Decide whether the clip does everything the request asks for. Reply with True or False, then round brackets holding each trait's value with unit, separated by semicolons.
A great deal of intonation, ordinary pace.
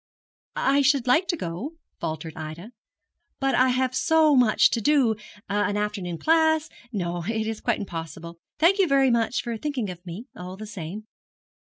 True (7.5 semitones; 170 wpm)